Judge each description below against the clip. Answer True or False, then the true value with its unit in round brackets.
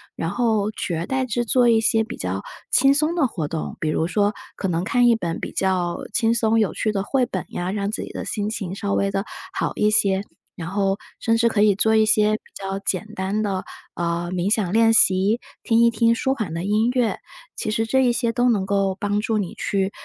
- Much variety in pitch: False (3.1 semitones)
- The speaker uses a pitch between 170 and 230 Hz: True (210 Hz)